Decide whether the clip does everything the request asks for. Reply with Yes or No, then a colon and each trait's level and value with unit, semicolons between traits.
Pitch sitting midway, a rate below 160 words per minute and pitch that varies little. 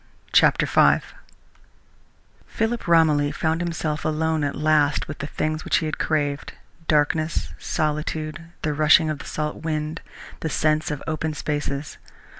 Yes: medium, 155 Hz; average, 140 wpm; narrow, 1.2 semitones